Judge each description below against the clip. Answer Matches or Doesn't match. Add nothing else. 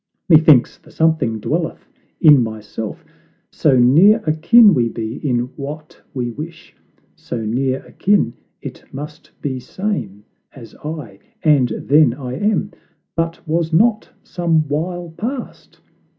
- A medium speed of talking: Doesn't match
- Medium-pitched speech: Matches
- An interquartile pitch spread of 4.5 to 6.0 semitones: Matches